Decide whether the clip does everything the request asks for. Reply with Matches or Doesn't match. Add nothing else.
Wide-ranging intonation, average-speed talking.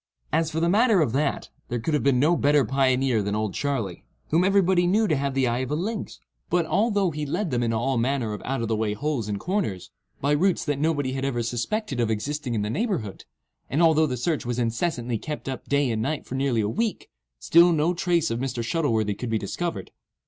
Doesn't match